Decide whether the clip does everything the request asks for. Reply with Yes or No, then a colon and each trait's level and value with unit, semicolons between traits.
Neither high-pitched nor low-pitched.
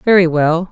Yes: medium, 175 Hz